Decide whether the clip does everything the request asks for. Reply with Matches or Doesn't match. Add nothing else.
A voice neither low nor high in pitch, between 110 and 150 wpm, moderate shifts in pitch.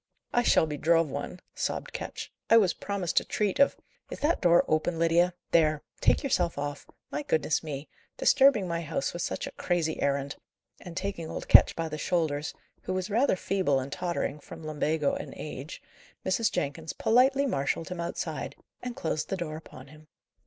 Doesn't match